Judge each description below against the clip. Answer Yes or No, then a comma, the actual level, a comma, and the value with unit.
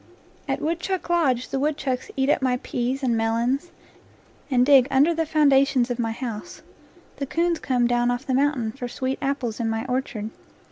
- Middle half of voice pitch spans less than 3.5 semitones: Yes, average, 2.9 semitones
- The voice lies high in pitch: Yes, very high, 260 Hz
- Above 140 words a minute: Yes, average, 180 wpm